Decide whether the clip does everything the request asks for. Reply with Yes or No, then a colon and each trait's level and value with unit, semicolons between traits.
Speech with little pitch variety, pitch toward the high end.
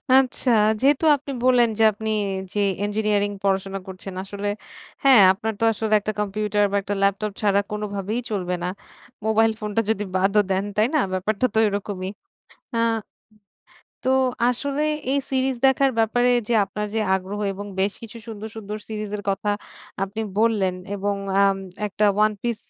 Yes: narrow, 2.2 semitones; high, 210 Hz